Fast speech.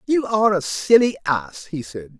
No: average, 190 wpm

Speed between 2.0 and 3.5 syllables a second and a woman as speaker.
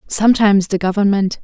No: 6.3 syllables/s; female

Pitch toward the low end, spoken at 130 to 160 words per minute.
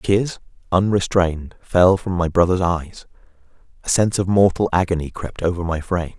Yes: very low, 90 Hz; average, 155 wpm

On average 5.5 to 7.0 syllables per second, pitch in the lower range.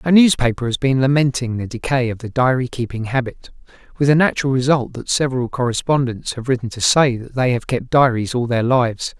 Yes: 5.8 syllables/s; low, 125 Hz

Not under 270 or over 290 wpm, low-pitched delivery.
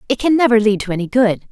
No: fast, 275 wpm; high, 230 Hz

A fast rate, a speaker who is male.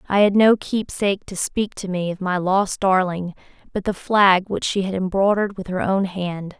No: fast, 210 wpm; female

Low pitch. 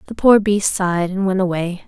No: high, 190 Hz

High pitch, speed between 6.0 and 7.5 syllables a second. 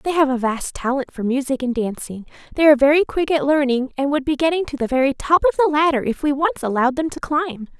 Yes: very high, 280 Hz; 6.3 syllables/s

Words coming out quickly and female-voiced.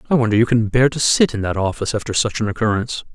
No: fast, 265 wpm; male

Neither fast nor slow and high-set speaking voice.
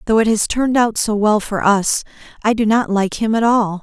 No: fast, 250 wpm; high, 215 Hz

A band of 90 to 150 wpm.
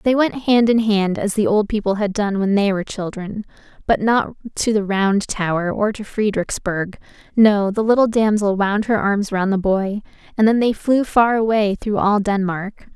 No: average, 200 wpm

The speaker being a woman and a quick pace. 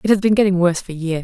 Yes: female; fast, 340 wpm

